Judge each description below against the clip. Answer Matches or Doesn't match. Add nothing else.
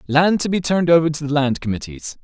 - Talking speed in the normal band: Doesn't match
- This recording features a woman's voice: Doesn't match